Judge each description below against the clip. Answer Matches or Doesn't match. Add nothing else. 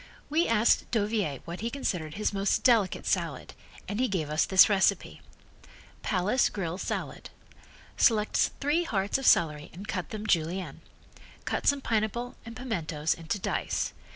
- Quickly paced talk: Doesn't match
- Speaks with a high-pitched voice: Matches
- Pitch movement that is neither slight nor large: Matches